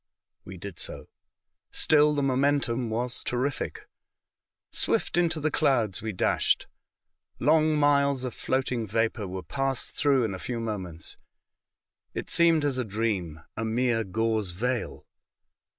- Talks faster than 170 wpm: No, slow, 135 wpm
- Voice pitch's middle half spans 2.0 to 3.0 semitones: No, average, 4.7 semitones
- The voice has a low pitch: Yes, low, 120 Hz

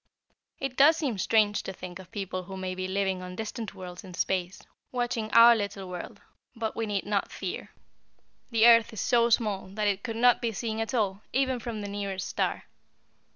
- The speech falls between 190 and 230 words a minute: Yes, average, 200 wpm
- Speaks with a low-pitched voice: No, high, 210 Hz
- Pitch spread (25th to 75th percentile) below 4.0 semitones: Yes, average, 3.4 semitones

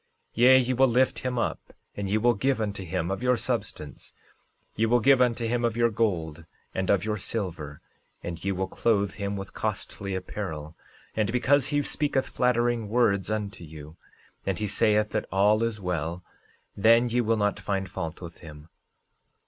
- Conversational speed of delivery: Yes, average, 180 wpm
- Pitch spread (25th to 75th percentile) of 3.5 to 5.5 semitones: Yes, average, 4.0 semitones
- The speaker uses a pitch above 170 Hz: No, low, 105 Hz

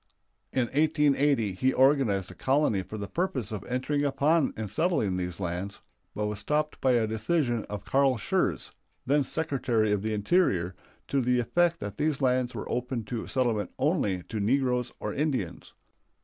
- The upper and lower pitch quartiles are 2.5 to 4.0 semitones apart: No, average, 5.3 semitones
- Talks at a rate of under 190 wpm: Yes, average, 165 wpm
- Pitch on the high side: No, low, 125 Hz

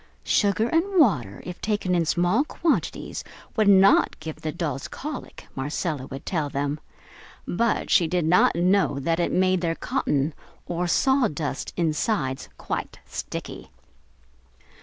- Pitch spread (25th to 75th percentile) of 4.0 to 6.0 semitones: Yes, average, 5.2 semitones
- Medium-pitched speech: Yes, medium, 175 Hz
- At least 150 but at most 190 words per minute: No, slow, 135 wpm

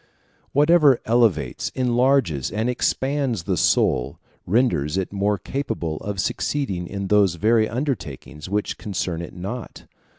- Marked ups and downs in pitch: Yes, wide, 5.8 semitones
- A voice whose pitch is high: No, low, 105 Hz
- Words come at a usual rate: No, slow, 125 wpm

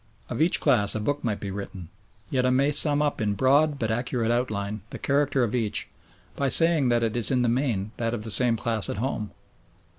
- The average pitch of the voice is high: No, low, 120 Hz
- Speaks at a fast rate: Yes, fast, 220 wpm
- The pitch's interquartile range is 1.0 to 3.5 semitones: No, average, 4.2 semitones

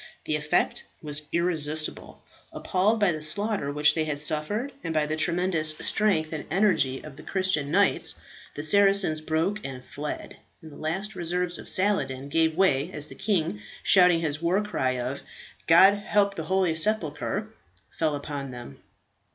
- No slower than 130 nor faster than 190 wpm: Yes, average, 160 wpm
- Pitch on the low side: No, medium, 160 Hz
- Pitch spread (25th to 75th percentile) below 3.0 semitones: No, average, 4.4 semitones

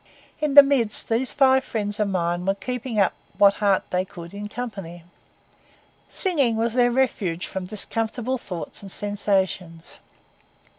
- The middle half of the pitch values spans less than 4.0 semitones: No, average, 4.6 semitones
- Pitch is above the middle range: Yes, high, 210 Hz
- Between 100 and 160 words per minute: Yes, average, 145 wpm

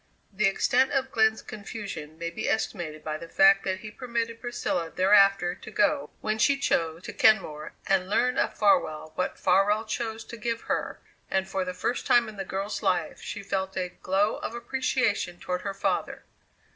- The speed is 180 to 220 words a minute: Yes, average, 185 wpm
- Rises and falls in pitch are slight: No, average, 3.5 semitones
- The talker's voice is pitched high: Yes, high, 200 Hz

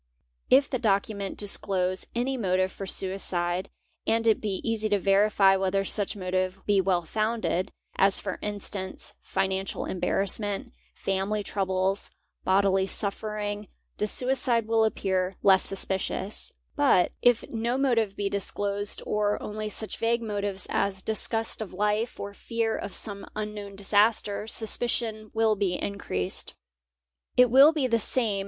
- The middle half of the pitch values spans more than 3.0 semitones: No, narrow, 2.4 semitones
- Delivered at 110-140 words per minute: Yes, slow, 135 wpm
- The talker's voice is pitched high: Yes, high, 205 Hz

